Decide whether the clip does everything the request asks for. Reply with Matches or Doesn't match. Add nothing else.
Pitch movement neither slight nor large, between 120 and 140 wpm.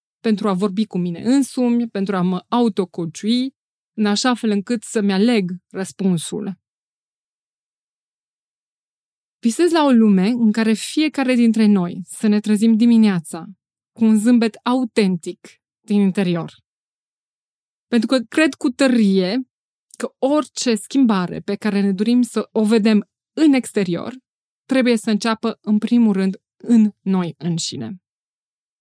Matches